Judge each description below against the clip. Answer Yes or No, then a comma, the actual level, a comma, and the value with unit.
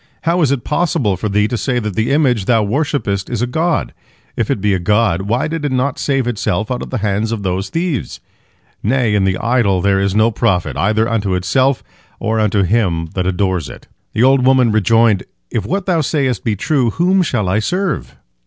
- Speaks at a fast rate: Yes, fast, 210 wpm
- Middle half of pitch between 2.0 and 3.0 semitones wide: No, average, 5.0 semitones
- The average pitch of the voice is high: No, low, 115 Hz